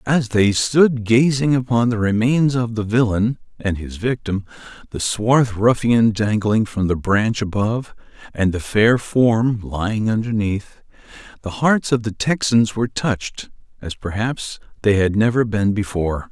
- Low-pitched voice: Yes, low, 110 Hz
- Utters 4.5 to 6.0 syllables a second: No, 4.3 syllables/s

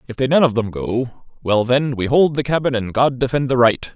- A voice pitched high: No, low, 125 Hz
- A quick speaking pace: Yes, fast, 260 wpm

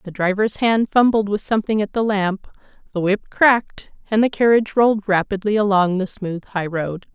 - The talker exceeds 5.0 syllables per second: Yes, 5.3 syllables/s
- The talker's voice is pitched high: Yes, high, 205 Hz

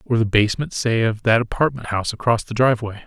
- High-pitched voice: No, low, 115 Hz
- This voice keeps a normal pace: No, fast, 215 wpm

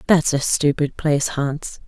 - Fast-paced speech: No, average, 160 wpm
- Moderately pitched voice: Yes, medium, 145 Hz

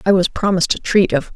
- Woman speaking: Yes, female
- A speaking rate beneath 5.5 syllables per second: No, 6.7 syllables/s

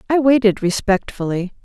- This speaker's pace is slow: Yes, slow, 110 wpm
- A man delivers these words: No, female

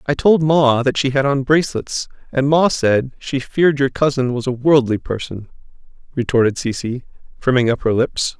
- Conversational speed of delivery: Yes, average, 180 wpm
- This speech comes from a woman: No, male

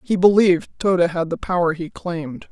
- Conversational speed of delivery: Yes, average, 190 wpm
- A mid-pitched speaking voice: Yes, medium, 175 Hz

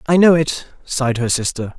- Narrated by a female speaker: No, male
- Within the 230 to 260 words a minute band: No, average, 200 wpm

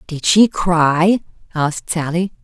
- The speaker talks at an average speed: No, slow, 125 wpm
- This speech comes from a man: No, female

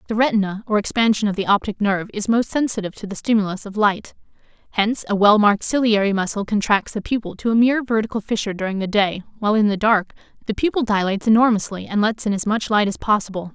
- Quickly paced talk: Yes, fast, 215 wpm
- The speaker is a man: No, female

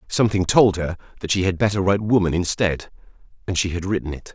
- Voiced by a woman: No, male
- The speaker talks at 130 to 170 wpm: No, fast, 205 wpm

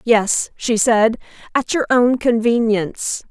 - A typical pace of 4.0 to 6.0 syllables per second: No, 3.7 syllables/s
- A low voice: No, high, 230 Hz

